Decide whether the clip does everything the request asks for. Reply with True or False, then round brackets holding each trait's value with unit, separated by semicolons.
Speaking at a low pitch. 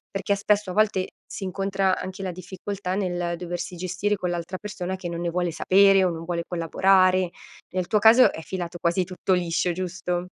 False (185 Hz)